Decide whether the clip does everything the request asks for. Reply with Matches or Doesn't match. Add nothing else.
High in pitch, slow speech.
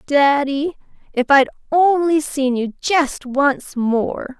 Matches